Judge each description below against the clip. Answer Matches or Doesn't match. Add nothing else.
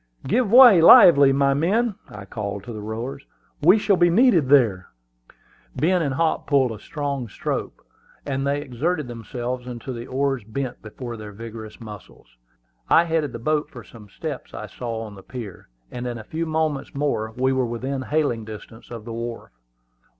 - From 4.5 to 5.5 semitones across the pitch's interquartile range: Matches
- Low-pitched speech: Matches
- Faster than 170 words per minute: Matches